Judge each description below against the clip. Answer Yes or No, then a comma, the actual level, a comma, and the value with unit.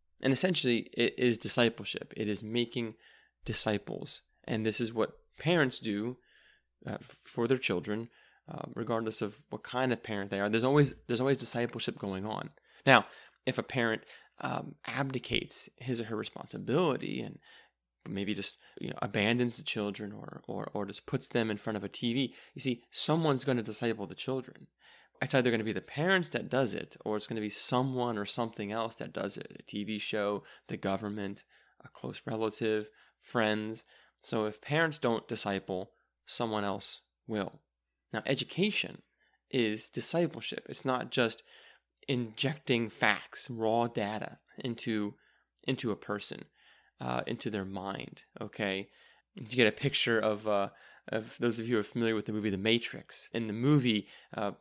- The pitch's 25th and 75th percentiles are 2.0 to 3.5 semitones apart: Yes, average, 3.1 semitones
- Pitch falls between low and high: No, low, 115 Hz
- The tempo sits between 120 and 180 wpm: Yes, average, 170 wpm